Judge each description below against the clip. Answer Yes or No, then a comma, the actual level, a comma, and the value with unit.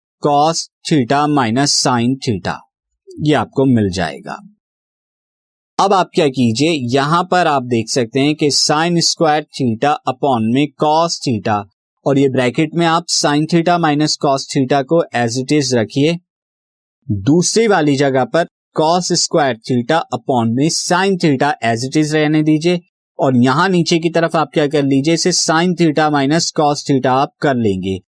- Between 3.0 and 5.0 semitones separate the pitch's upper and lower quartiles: Yes, average, 4.3 semitones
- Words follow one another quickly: No, average, 160 wpm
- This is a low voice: No, medium, 145 Hz